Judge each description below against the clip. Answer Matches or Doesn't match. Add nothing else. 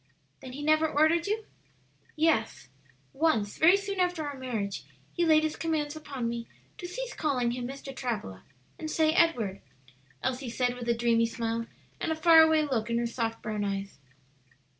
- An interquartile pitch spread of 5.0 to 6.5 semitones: Matches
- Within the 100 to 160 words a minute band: Doesn't match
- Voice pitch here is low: Doesn't match